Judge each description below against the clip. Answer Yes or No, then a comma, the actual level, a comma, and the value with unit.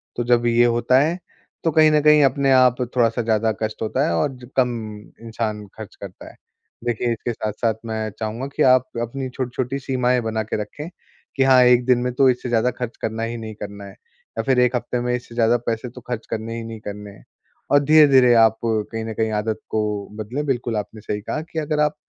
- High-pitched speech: No, low, 120 Hz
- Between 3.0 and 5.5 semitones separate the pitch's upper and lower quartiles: No, narrow, 2.6 semitones